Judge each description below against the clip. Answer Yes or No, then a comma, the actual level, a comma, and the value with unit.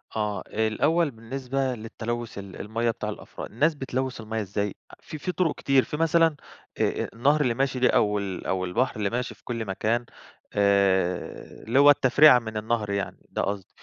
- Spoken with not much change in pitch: No, average, 4.6 semitones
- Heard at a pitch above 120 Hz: No, low, 115 Hz